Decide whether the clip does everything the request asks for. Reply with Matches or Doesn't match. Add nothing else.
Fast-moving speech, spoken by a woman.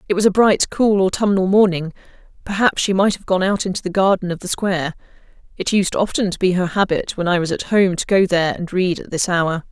Matches